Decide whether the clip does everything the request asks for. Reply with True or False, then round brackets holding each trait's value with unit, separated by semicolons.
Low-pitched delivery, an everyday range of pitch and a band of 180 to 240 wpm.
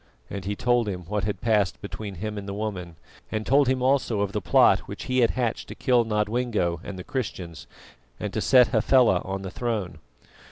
True (105 Hz; 3.9 semitones; 205 wpm)